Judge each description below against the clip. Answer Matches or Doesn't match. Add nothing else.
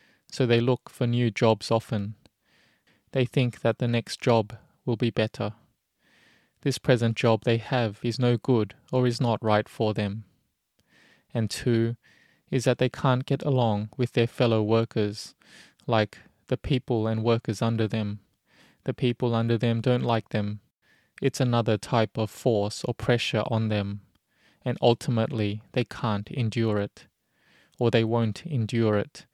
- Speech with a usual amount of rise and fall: Doesn't match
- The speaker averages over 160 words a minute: Doesn't match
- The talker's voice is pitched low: Matches